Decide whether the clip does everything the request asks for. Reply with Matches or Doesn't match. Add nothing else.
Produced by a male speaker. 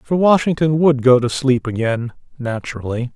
Matches